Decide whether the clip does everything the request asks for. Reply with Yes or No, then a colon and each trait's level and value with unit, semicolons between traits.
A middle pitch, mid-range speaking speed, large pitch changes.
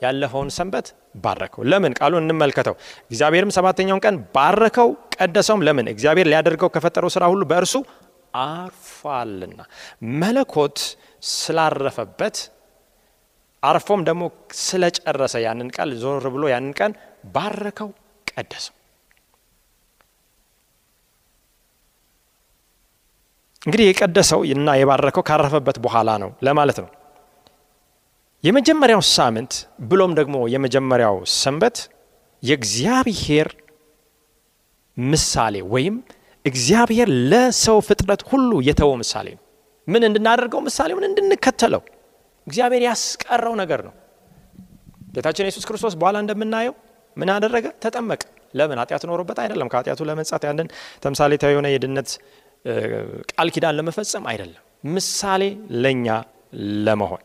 Yes: medium, 170 Hz; average, 95 wpm; wide, 7.4 semitones